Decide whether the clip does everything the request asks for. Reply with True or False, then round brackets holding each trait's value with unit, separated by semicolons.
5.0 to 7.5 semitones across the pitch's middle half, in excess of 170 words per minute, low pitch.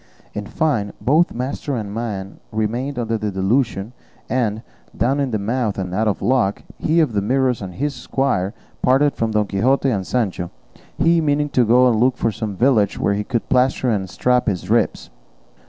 False (4.3 semitones; 185 wpm; 115 Hz)